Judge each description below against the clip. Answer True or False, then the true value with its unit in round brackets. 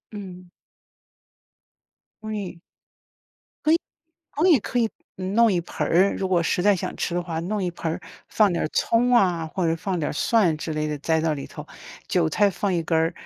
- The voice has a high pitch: False (180 Hz)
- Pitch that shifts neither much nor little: True (4.0 semitones)